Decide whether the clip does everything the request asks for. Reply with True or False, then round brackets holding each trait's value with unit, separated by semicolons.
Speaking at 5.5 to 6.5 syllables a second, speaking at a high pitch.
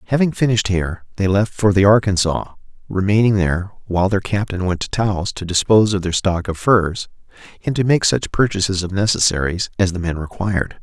False (5.8 syllables/s; 95 Hz)